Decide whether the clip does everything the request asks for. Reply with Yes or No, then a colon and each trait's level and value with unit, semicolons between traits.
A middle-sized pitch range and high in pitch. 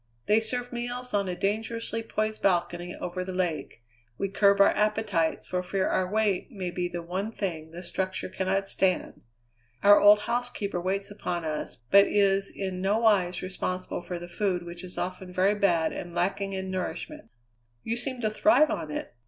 Yes: average, 3.0 semitones; high, 195 Hz